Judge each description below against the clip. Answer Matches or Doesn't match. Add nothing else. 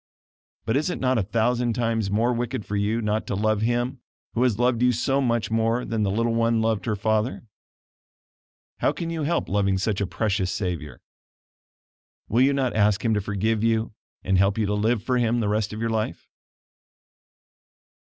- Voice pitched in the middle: Doesn't match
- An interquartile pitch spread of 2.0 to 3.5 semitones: Matches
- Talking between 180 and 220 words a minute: Matches